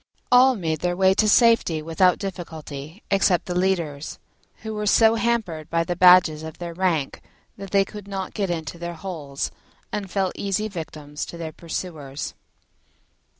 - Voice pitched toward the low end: No, medium, 180 Hz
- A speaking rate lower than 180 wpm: Yes, average, 160 wpm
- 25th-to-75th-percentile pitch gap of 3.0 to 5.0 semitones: Yes, average, 3.7 semitones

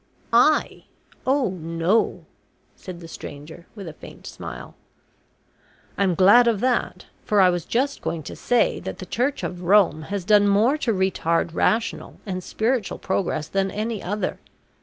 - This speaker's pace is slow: No, average, 155 wpm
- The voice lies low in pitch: No, high, 195 Hz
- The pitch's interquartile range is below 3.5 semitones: No, average, 4.3 semitones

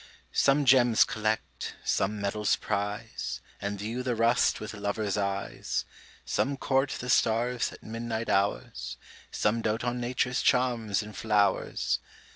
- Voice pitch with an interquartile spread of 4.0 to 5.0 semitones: No, average, 3.0 semitones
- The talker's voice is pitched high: No, low, 110 Hz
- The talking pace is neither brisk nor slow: No, slow, 130 wpm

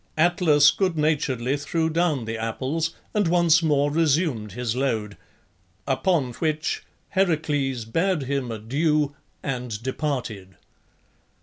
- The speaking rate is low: Yes, slow, 110 wpm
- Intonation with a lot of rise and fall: No, average, 4.7 semitones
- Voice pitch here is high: No, medium, 145 Hz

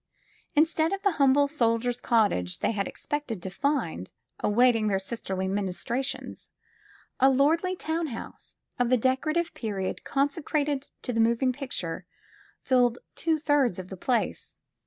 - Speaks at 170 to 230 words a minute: No, average, 140 wpm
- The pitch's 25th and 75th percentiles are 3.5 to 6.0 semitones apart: Yes, average, 5.2 semitones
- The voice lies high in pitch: Yes, very high, 255 Hz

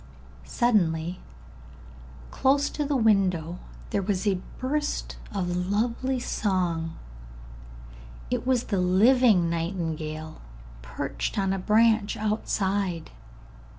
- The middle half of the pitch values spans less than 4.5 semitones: No, average, 4.8 semitones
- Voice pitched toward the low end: No, high, 195 Hz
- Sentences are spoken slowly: Yes, slow, 95 wpm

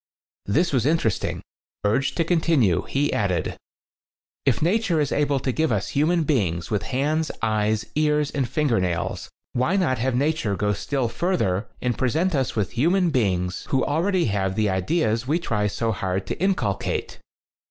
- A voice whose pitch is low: Yes, low, 130 Hz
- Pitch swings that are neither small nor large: No, wide, 7.1 semitones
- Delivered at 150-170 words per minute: Yes, average, 165 wpm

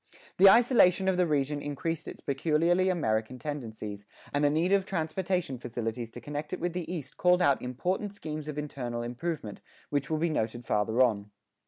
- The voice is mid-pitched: Yes, medium, 150 Hz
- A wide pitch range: Yes, wide, 6.3 semitones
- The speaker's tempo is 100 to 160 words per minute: No, average, 180 wpm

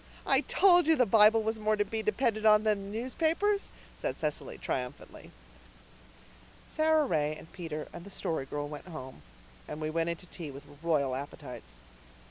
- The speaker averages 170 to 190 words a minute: Yes, average, 175 wpm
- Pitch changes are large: Yes, wide, 6.6 semitones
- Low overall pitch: No, high, 195 Hz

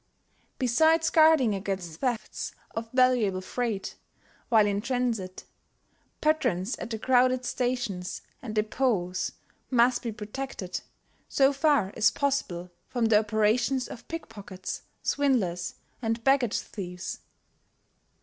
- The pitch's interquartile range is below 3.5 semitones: No, average, 4.3 semitones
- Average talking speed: No, slow, 110 wpm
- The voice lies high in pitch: Yes, high, 230 Hz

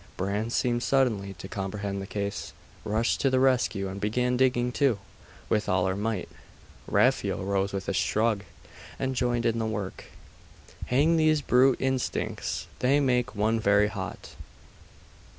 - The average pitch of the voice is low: Yes, low, 115 Hz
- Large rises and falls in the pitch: No, average, 4.1 semitones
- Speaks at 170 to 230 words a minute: No, average, 150 wpm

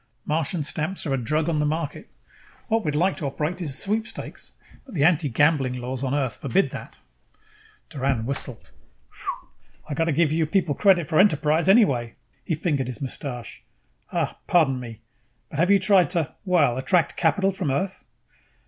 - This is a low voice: No, medium, 155 Hz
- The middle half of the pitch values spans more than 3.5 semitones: Yes, average, 4.7 semitones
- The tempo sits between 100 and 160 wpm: No, average, 175 wpm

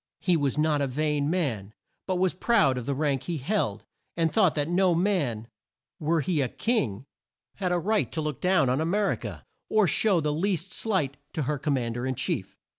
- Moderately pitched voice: Yes, medium, 155 Hz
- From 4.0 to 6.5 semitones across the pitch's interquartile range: Yes, average, 5.3 semitones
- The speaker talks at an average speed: No, fast, 215 wpm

